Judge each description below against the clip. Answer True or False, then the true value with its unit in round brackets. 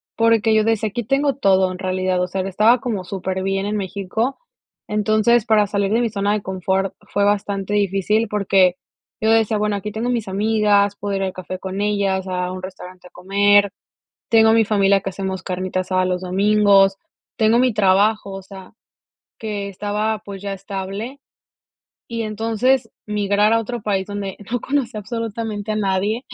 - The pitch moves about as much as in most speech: False (2.3 semitones)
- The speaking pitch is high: True (205 Hz)